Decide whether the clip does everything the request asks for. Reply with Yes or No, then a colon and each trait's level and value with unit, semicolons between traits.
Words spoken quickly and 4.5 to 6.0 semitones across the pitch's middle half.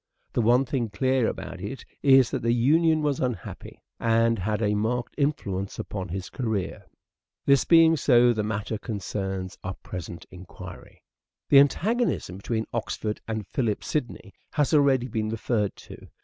No: average, 150 wpm; average, 4.8 semitones